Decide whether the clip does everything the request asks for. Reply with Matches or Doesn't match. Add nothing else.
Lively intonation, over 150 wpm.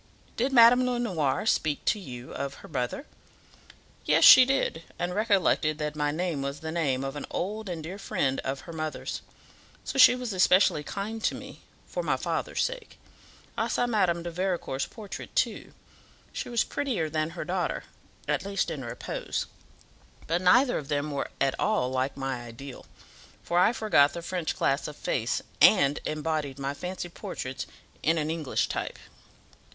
Matches